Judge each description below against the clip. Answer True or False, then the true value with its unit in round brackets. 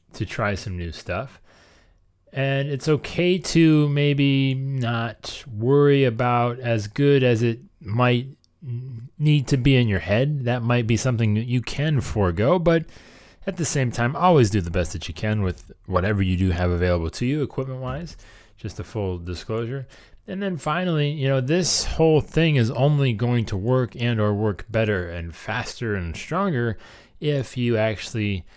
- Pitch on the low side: True (120 Hz)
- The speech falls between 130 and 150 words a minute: False (170 wpm)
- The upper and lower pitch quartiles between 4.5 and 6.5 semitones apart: True (5.1 semitones)